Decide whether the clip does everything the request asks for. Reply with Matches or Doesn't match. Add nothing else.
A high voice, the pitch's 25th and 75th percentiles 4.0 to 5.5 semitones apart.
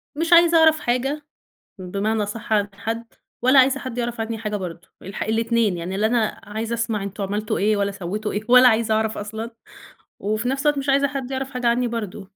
Doesn't match